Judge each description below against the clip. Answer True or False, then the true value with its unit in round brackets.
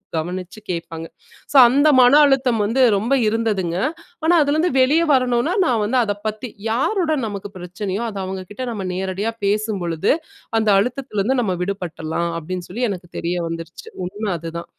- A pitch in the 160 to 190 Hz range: False (205 Hz)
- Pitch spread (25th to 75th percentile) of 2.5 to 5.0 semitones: False (5.5 semitones)